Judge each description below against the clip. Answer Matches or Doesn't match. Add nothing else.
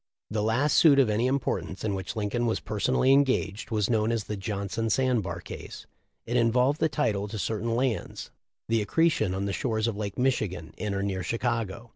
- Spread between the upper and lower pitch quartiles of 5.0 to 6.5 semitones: Doesn't match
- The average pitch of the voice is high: Doesn't match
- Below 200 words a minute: Doesn't match